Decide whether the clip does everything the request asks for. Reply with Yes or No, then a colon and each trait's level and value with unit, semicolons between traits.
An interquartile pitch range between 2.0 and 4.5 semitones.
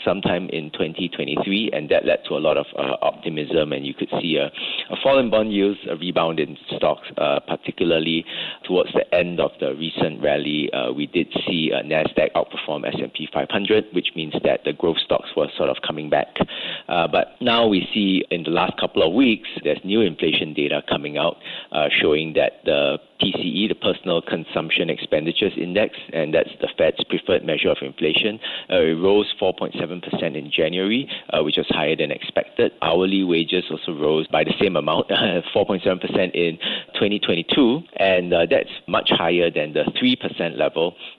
Yes: average, 4.1 semitones